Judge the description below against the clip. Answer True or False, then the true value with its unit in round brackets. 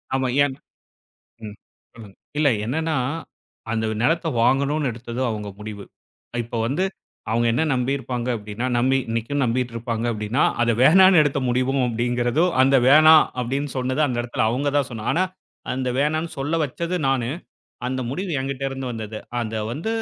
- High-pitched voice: False (130 Hz)